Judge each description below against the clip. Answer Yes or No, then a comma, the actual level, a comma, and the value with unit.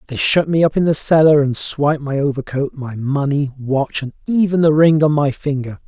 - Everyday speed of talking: No, fast, 215 wpm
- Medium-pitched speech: Yes, medium, 145 Hz